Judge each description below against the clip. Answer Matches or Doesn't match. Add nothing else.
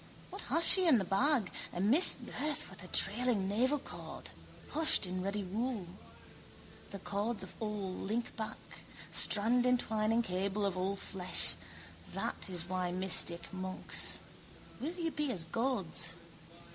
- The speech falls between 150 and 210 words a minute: Doesn't match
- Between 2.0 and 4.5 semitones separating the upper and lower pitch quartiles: Doesn't match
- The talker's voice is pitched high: Matches